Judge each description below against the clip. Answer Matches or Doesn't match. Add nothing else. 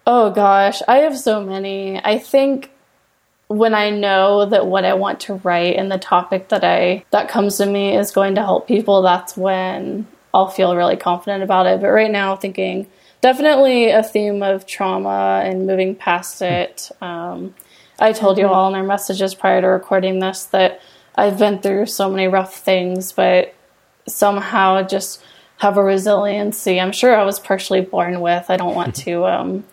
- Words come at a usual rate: Matches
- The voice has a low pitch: Doesn't match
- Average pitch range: Doesn't match